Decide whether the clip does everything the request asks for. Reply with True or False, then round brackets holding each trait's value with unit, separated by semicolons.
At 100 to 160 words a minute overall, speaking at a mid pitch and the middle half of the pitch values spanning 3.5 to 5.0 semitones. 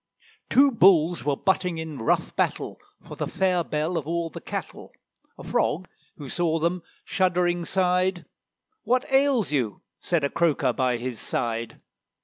True (150 wpm; 170 Hz; 3.8 semitones)